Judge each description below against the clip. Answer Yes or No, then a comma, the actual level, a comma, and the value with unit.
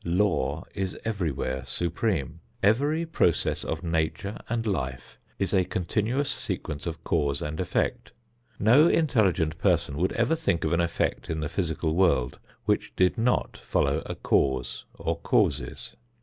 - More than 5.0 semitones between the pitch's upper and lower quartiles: Yes, wide, 5.6 semitones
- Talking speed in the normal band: Yes, average, 145 wpm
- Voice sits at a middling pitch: No, very low, 85 Hz